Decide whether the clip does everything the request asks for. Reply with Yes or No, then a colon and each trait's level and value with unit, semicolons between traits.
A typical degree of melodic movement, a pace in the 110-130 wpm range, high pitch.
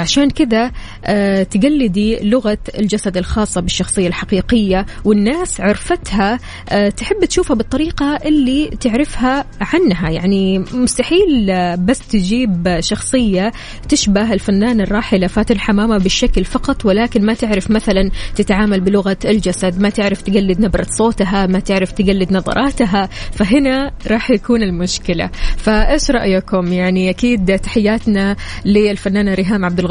Yes: average, 4.0 semitones; average, 115 wpm; high, 210 Hz